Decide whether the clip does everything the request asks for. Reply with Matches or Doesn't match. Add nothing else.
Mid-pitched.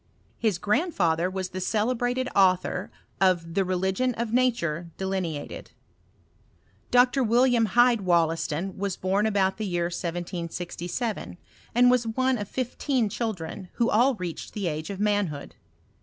Doesn't match